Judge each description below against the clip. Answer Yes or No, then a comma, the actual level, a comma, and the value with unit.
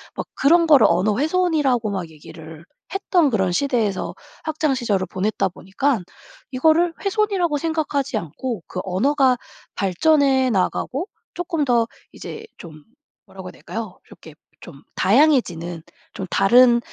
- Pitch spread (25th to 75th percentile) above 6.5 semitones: Yes, wide, 8.4 semitones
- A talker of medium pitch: No, very high, 250 Hz